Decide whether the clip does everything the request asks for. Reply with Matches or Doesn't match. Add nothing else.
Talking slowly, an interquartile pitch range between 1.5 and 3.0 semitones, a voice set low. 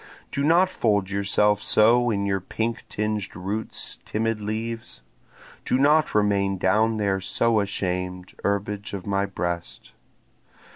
Matches